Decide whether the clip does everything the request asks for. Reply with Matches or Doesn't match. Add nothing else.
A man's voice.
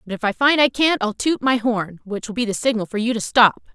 Doesn't match